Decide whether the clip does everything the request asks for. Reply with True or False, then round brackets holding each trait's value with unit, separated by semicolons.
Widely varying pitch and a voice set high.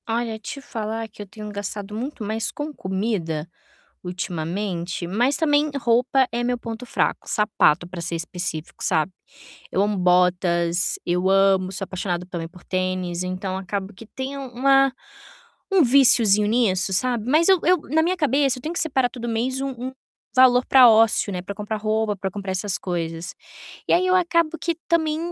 True (5.8 semitones; 215 Hz)